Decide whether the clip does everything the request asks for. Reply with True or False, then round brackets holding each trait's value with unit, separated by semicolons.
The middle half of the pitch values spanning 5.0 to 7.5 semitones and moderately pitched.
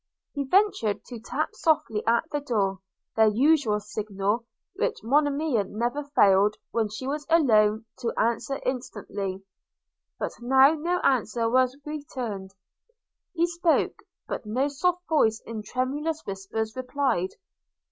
False (5.4 semitones; 245 Hz)